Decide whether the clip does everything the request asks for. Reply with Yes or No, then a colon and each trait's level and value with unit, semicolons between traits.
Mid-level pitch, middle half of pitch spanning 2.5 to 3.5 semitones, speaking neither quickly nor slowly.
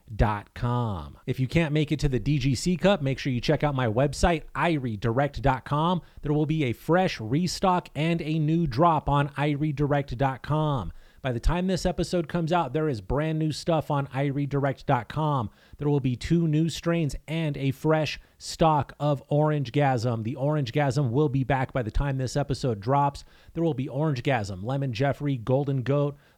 Yes: medium, 145 Hz; average, 2.9 semitones; average, 180 wpm